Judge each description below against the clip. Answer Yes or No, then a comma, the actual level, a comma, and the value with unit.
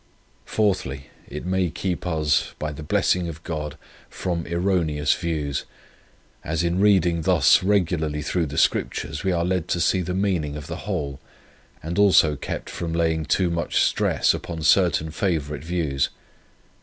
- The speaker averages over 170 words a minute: No, average, 155 wpm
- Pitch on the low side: Yes, very low, 85 Hz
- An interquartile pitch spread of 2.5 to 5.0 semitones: Yes, average, 2.8 semitones